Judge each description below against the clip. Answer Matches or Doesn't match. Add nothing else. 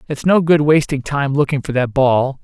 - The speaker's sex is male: Matches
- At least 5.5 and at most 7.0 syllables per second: Doesn't match